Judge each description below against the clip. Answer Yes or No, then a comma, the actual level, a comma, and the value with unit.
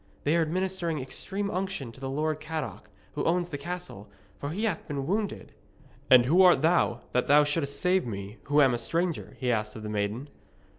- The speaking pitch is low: No, medium, 150 Hz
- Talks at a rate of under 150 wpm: No, average, 200 wpm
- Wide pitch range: Yes, wide, 5.7 semitones